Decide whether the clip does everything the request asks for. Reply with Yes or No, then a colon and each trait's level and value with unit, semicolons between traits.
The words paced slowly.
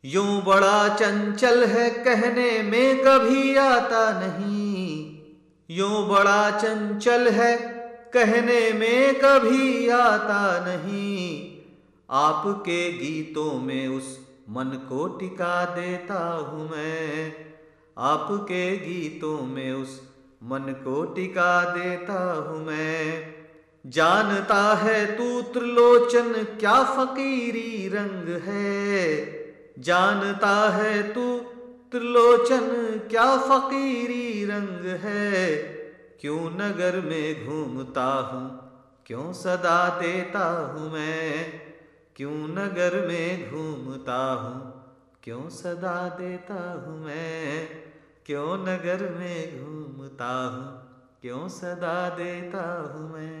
Yes: slow, 95 wpm